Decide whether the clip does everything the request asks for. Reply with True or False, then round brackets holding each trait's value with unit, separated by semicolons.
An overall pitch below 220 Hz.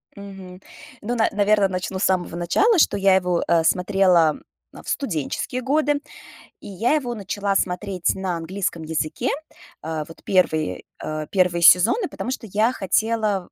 True (190 Hz)